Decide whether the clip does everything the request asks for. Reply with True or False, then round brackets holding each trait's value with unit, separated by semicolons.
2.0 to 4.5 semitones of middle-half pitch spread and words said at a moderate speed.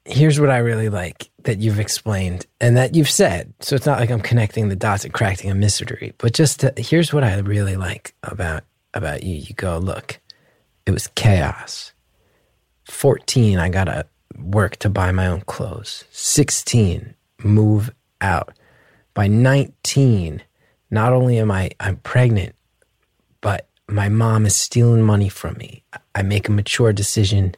True (3.6 semitones; 165 wpm)